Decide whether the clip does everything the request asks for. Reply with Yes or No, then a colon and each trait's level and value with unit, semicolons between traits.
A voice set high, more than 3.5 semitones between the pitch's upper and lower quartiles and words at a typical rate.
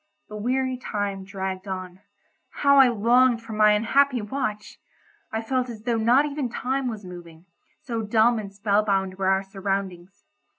Yes: high, 215 Hz; average, 4.1 semitones; average, 165 wpm